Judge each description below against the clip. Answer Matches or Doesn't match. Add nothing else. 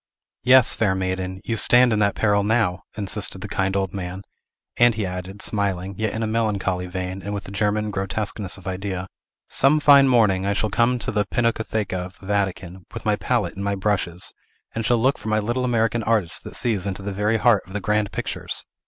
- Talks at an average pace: Doesn't match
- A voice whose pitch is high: Doesn't match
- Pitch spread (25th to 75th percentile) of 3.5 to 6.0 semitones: Doesn't match